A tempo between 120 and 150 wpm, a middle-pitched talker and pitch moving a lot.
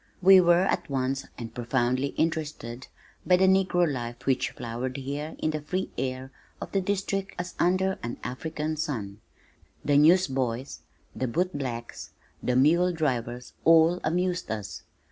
Yes: average, 140 wpm; medium, 145 Hz; wide, 5.8 semitones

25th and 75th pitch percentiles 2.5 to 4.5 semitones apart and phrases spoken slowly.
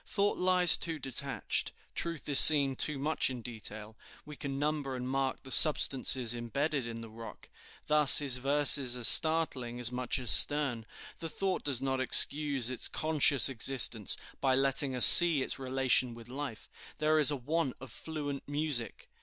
No: average, 3.3 semitones; average, 170 wpm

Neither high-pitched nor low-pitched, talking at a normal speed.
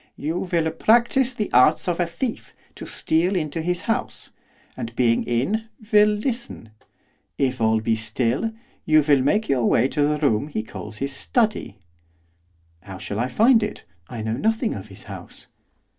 Yes: medium, 155 Hz; average, 170 wpm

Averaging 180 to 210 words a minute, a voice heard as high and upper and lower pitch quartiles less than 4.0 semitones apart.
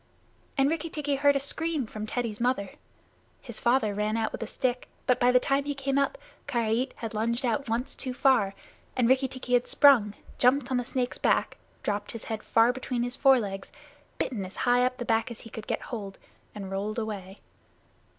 Yes: average, 200 wpm; high, 245 Hz; average, 3.5 semitones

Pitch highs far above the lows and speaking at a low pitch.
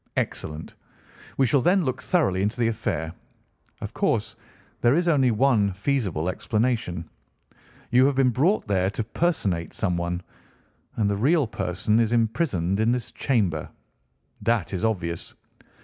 Yes: wide, 6.0 semitones; low, 110 Hz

